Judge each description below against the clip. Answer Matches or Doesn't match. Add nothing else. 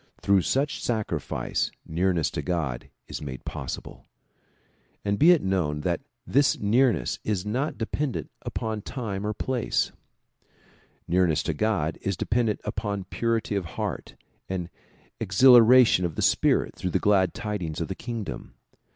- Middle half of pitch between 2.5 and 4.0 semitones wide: Doesn't match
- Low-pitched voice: Matches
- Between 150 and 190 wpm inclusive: Doesn't match